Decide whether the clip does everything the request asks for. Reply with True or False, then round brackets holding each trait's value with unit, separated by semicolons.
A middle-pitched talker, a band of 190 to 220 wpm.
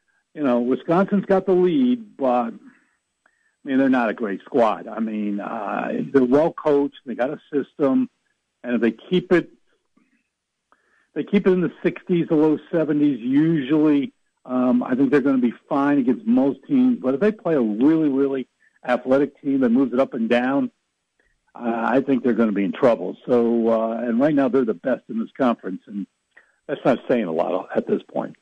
True (150 Hz; 200 wpm)